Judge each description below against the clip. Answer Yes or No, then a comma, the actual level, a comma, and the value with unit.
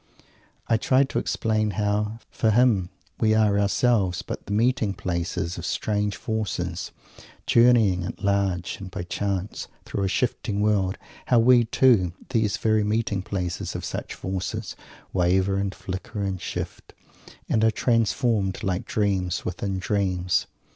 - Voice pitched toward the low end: Yes, low, 100 Hz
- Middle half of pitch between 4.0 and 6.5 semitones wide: No, average, 2.9 semitones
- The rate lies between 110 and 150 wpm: Yes, average, 140 wpm